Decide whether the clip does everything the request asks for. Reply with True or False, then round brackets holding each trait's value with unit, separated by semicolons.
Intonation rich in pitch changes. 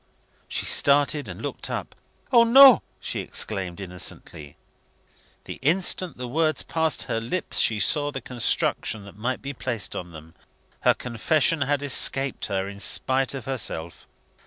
True (6.5 semitones)